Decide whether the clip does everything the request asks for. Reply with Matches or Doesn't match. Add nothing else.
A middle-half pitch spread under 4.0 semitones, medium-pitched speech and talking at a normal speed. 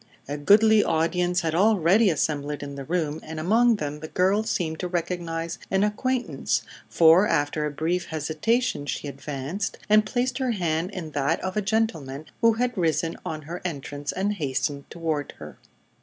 Doesn't match